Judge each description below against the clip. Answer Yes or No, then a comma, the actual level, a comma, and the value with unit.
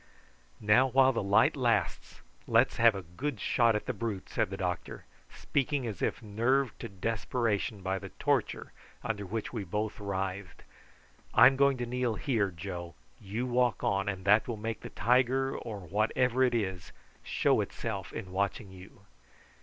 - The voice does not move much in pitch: No, average, 4.1 semitones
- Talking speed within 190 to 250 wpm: No, average, 165 wpm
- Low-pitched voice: Yes, low, 110 Hz